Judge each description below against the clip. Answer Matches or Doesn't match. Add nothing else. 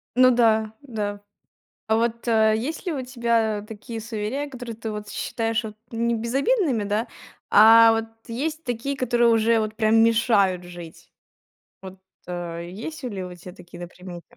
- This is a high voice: Matches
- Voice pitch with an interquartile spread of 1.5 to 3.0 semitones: Matches